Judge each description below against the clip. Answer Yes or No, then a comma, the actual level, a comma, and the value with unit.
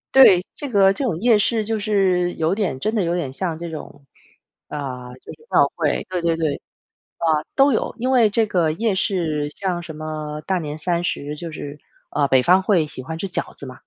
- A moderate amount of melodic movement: Yes, average, 4.9 semitones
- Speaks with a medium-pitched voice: Yes, medium, 170 Hz